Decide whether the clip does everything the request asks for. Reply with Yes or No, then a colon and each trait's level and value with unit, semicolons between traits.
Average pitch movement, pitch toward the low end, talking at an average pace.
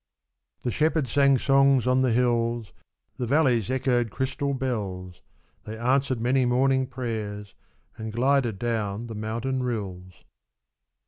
No: average, 3.1 semitones; low, 120 Hz; slow, 125 wpm